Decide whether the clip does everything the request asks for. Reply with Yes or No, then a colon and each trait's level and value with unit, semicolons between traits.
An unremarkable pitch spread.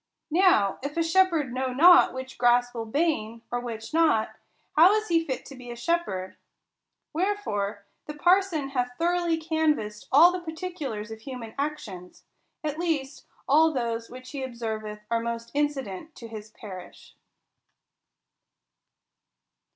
No: wide, 6.1 semitones